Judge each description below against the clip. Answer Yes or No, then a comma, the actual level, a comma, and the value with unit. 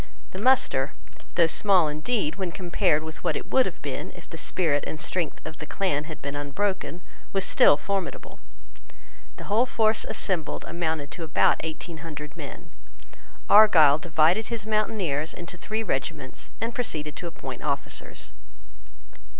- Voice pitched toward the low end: No, medium, 165 Hz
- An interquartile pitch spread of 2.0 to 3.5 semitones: No, average, 4.8 semitones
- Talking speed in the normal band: Yes, average, 150 wpm